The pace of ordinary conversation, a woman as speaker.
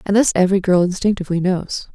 Yes: average, 185 wpm; female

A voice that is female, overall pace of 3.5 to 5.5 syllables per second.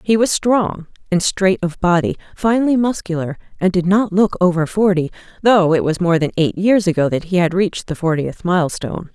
Yes: female; 5.4 syllables/s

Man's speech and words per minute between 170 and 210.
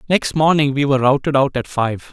No: male; fast, 225 wpm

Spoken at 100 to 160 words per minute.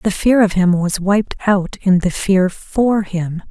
No: fast, 205 wpm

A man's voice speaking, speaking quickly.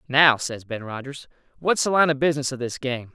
Yes: male; fast, 230 wpm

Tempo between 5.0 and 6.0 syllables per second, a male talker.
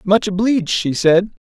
No: 4.8 syllables/s; male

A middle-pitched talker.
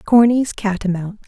No: high, 210 Hz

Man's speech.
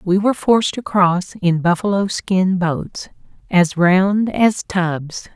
No: female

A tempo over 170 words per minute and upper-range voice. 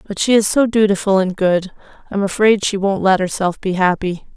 Yes: fast, 205 wpm; high, 195 Hz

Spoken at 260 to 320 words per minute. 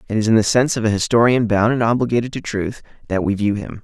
Yes: fast, 265 wpm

